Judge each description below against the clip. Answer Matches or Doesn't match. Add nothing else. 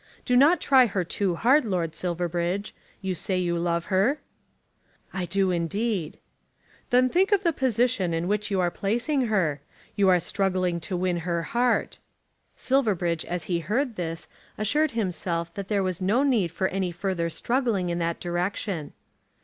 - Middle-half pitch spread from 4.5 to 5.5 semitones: Matches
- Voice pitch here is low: Doesn't match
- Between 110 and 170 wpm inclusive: Matches